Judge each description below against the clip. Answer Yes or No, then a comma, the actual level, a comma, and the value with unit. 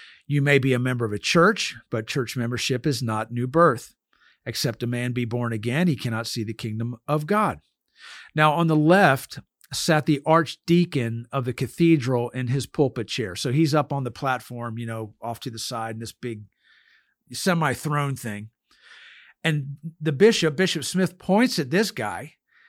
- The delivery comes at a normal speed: Yes, average, 180 wpm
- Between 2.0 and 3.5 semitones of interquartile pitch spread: No, average, 5.1 semitones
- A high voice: No, low, 130 Hz